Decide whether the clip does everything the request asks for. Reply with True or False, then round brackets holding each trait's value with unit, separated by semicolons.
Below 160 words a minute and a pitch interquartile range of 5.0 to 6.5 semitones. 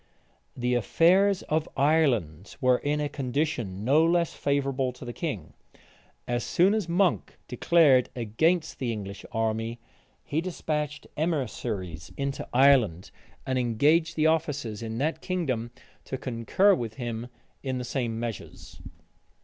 True (135 wpm; 5.4 semitones)